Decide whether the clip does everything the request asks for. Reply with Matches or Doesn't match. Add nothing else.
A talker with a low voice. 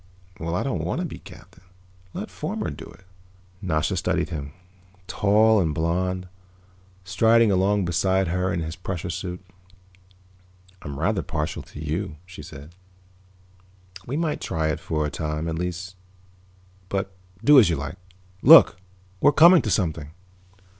Matches